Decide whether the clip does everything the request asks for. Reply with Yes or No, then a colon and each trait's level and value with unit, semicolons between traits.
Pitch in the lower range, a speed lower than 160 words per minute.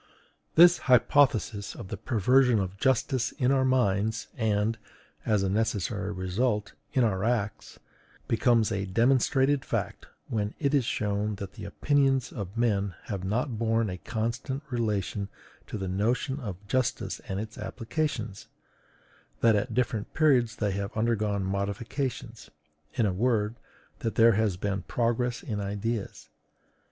Yes: low, 110 Hz; average, 140 wpm